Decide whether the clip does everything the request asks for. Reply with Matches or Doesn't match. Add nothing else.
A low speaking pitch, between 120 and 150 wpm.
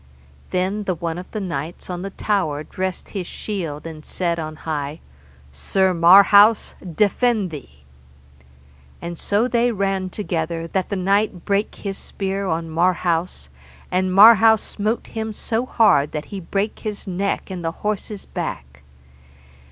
Doesn't match